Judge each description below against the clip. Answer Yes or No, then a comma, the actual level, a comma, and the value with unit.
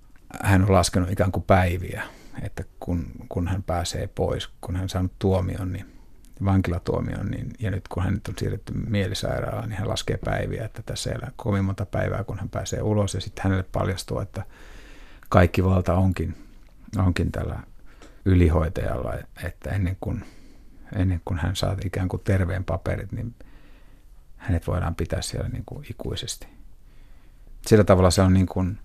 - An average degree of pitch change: Yes, average, 3.0 semitones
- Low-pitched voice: Yes, very low, 95 Hz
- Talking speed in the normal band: No, fast, 160 wpm